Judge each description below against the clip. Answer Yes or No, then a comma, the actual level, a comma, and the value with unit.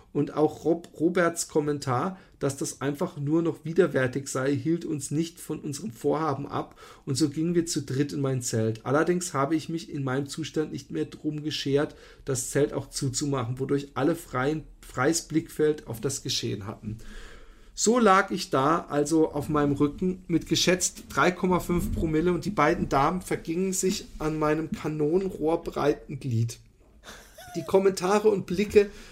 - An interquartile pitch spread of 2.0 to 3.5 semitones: Yes, average, 3.2 semitones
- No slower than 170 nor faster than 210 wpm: No, average, 160 wpm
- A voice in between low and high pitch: Yes, medium, 155 Hz